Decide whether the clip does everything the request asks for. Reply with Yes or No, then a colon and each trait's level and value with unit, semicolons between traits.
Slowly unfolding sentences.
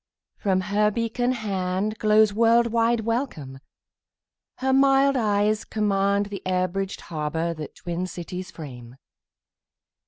Yes: slow, 105 wpm